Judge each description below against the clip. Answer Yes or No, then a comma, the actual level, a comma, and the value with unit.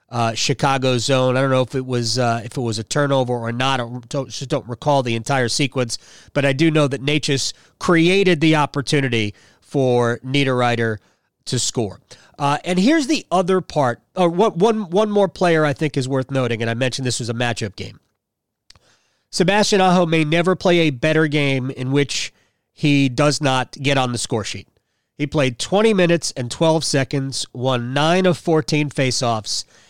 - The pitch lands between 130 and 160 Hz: Yes, low, 135 Hz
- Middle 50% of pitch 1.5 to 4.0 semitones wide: No, average, 4.5 semitones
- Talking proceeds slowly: No, average, 190 wpm